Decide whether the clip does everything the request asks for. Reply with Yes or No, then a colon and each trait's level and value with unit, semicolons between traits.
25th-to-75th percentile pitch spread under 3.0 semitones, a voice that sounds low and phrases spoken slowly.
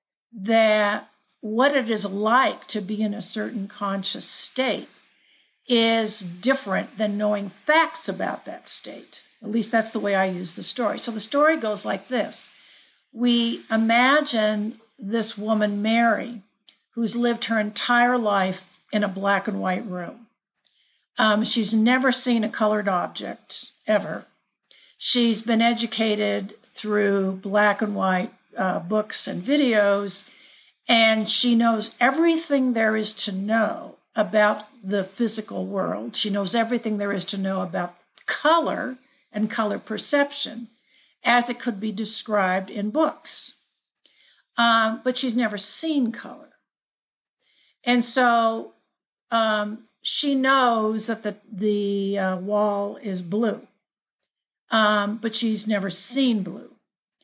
No: narrow, 2.5 semitones; high, 220 Hz; slow, 130 wpm